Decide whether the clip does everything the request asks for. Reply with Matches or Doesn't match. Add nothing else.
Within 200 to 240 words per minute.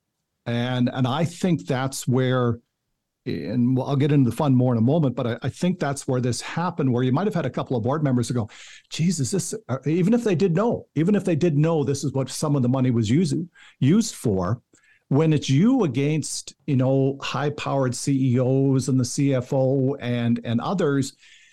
Matches